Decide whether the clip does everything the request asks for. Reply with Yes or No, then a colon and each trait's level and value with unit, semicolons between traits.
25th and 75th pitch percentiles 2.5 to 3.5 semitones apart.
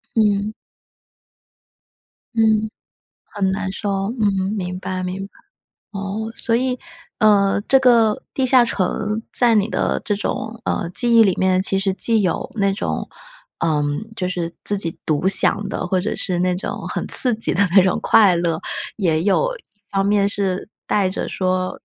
Yes: average, 2.9 semitones